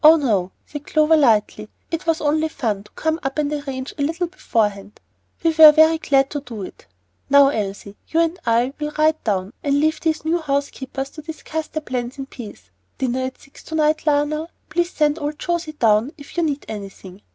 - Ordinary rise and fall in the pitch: Yes, average, 4.6 semitones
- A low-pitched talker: No, very high, 290 Hz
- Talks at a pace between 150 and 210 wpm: Yes, fast, 205 wpm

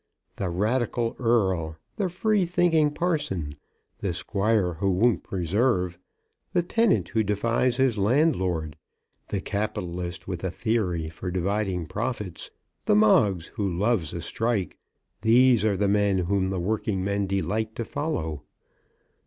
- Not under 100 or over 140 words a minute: Yes, slow, 135 wpm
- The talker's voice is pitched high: No, low, 100 Hz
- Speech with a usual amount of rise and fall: Yes, average, 4.7 semitones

